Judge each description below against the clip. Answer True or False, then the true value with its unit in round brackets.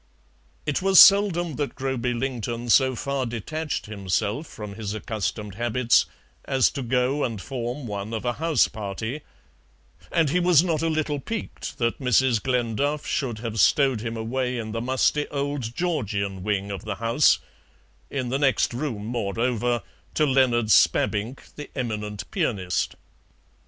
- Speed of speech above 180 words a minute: False (150 wpm)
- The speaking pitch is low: True (125 Hz)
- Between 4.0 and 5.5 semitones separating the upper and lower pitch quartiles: True (4.4 semitones)